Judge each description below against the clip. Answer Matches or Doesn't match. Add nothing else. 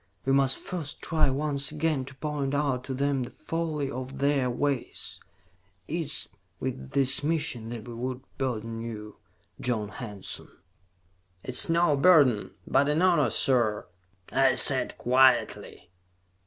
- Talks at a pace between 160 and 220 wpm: Doesn't match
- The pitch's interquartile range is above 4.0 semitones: Doesn't match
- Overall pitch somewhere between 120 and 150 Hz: Matches